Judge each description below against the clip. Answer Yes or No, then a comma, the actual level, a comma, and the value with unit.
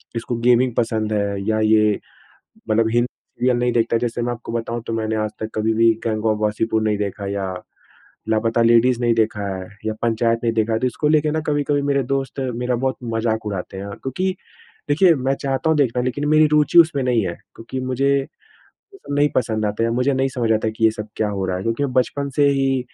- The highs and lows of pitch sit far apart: No, average, 3.3 semitones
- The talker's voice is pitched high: No, low, 115 Hz